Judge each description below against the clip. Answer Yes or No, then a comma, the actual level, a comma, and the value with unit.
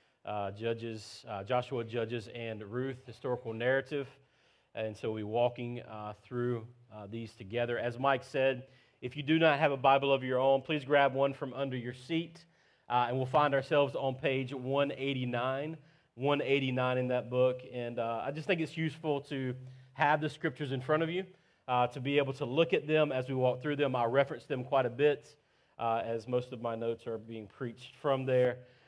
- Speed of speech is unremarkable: Yes, average, 195 wpm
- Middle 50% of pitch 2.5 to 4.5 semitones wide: Yes, average, 2.9 semitones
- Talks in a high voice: No, low, 130 Hz